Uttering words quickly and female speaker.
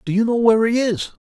No: fast, 295 wpm; male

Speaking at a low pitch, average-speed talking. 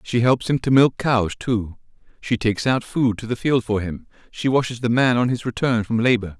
No: low, 120 Hz; fast, 235 wpm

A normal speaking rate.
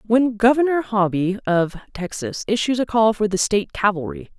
Yes: average, 165 wpm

